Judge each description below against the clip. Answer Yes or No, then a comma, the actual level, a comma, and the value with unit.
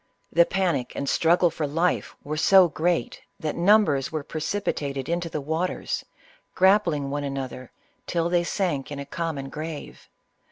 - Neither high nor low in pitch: Yes, medium, 160 Hz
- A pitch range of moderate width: Yes, average, 3.6 semitones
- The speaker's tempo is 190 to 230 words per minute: No, average, 150 wpm